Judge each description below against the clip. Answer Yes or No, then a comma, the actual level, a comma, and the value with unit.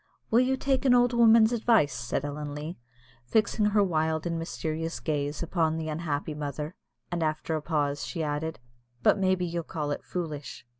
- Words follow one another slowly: No, average, 180 wpm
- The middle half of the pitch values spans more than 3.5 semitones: Yes, average, 4.5 semitones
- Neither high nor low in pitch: Yes, medium, 160 Hz